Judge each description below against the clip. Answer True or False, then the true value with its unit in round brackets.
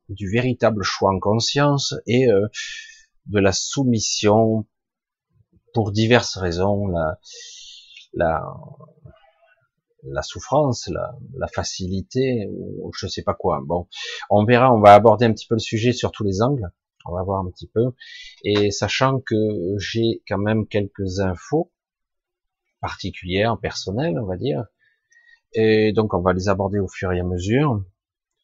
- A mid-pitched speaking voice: False (110 Hz)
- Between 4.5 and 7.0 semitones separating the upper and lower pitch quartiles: True (5.2 semitones)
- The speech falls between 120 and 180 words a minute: True (150 wpm)